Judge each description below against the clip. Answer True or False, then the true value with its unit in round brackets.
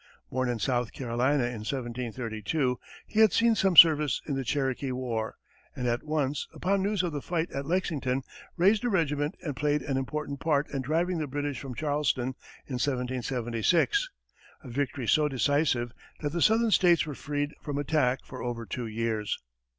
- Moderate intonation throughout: True (3.9 semitones)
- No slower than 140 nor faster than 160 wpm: False (175 wpm)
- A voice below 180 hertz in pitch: True (140 Hz)